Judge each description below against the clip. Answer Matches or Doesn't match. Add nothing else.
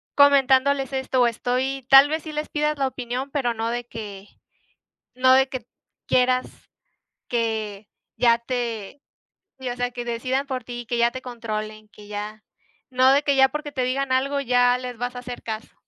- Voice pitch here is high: Matches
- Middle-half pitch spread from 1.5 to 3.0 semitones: Matches